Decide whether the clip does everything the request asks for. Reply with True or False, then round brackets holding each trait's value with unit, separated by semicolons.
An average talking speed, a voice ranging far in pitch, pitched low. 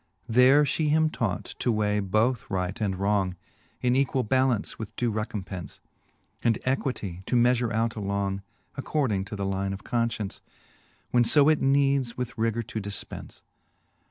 False (155 wpm; 4.2 semitones; 115 Hz)